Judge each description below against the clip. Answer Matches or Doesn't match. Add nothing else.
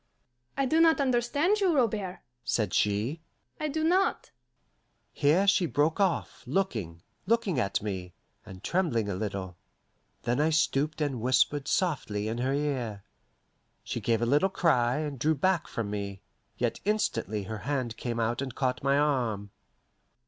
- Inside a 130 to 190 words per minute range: Matches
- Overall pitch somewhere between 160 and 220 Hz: Doesn't match